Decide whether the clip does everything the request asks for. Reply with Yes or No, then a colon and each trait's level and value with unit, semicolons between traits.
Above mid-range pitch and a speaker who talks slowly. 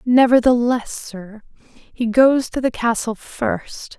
Yes: high, 240 Hz; slow, 120 wpm